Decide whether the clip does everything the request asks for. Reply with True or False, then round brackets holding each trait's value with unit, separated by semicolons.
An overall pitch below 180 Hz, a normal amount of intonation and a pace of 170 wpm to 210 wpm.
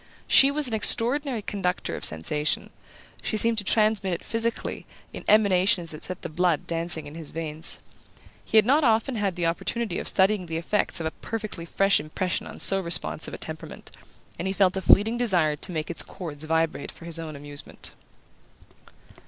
False (185 Hz; 4.9 semitones; 185 wpm)